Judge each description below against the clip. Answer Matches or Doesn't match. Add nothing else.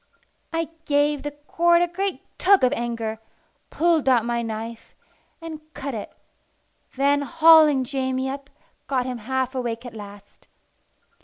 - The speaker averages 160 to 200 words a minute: Doesn't match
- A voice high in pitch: Matches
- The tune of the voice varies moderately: Matches